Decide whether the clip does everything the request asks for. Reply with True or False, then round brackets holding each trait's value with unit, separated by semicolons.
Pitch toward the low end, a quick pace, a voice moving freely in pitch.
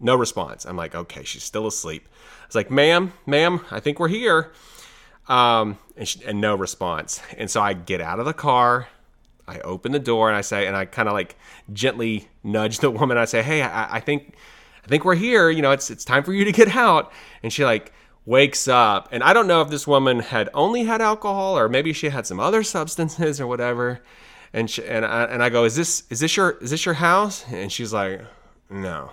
True (125 Hz; 230 wpm; 6.4 semitones)